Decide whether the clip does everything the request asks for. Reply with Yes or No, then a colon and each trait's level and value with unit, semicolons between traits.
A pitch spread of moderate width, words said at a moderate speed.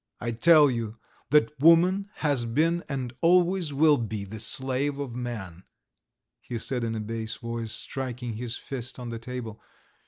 Yes: average, 4.3 semitones; average, 160 wpm